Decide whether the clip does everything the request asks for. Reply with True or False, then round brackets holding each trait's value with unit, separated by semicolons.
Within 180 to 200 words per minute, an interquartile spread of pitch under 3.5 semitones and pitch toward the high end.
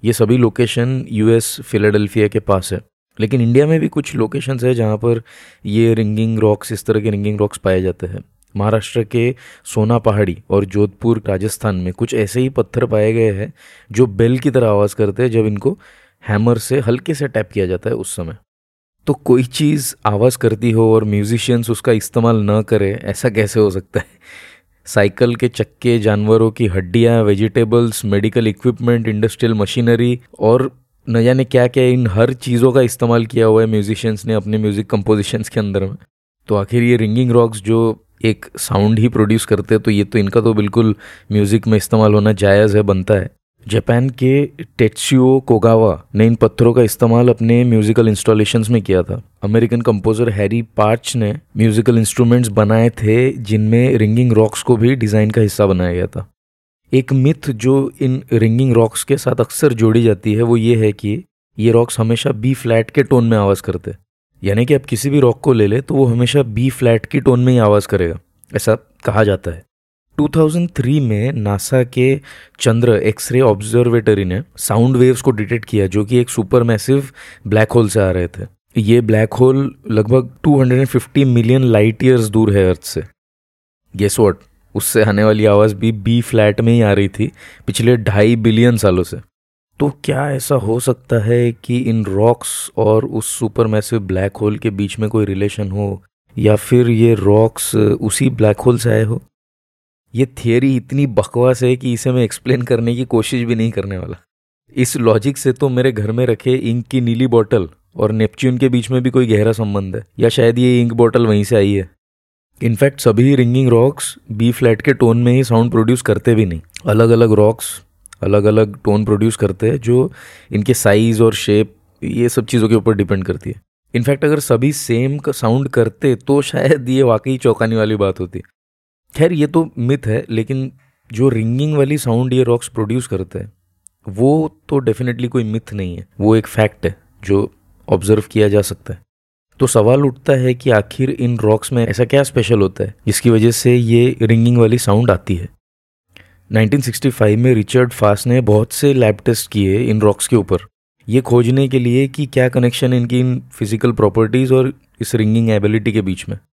False (190 wpm; 2.9 semitones; 115 Hz)